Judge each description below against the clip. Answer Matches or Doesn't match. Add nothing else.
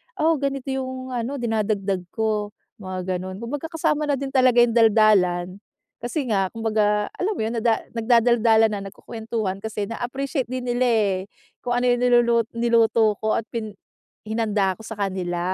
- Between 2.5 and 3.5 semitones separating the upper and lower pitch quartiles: Matches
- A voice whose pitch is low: Doesn't match